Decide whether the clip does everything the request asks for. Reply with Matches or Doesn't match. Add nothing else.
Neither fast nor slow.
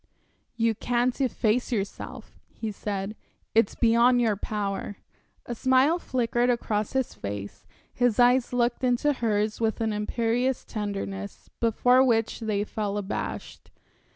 Doesn't match